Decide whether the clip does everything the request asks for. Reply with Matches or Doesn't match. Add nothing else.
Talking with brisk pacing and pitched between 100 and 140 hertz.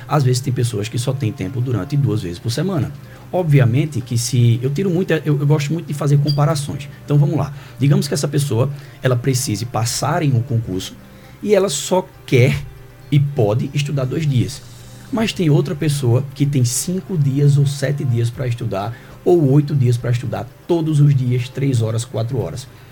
Matches